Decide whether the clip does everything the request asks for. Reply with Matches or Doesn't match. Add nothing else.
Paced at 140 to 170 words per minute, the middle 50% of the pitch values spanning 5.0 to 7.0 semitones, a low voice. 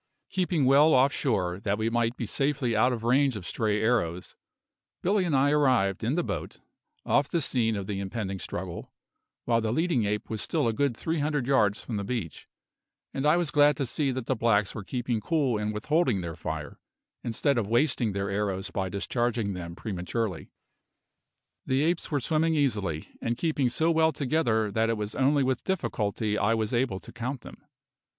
Doesn't match